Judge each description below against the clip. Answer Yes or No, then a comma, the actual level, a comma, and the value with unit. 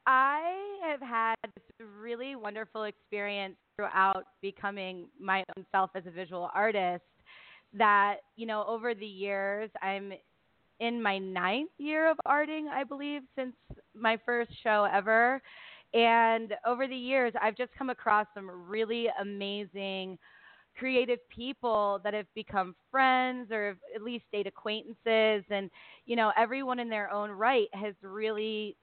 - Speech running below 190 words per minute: Yes, average, 145 wpm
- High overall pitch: Yes, high, 215 Hz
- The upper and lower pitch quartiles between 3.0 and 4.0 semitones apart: Yes, average, 3.4 semitones